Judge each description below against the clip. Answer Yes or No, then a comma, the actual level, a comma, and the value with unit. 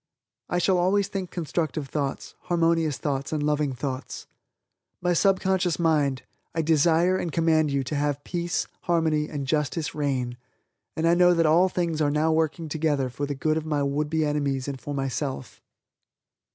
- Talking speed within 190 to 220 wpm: No, average, 165 wpm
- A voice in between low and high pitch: Yes, medium, 155 Hz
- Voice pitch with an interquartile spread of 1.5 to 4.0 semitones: Yes, average, 2.8 semitones